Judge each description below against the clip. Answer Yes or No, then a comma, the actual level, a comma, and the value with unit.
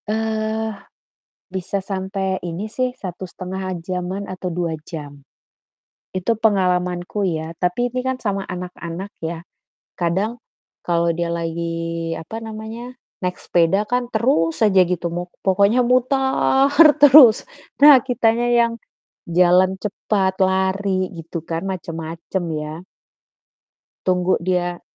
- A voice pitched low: No, high, 190 Hz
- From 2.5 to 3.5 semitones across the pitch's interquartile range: No, average, 4.2 semitones